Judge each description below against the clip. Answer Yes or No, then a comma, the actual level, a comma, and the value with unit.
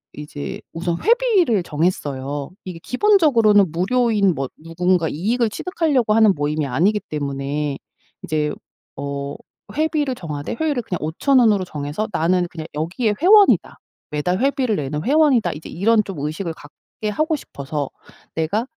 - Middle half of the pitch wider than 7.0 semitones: Yes, wide, 8.2 semitones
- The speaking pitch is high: No, medium, 180 Hz